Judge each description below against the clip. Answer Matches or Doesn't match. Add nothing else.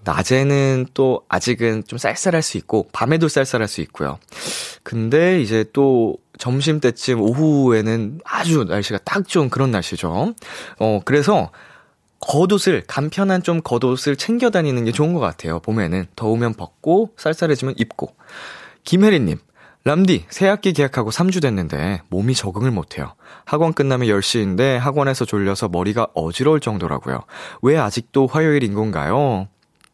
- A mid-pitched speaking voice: Doesn't match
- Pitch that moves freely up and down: Matches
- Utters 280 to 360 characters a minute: Matches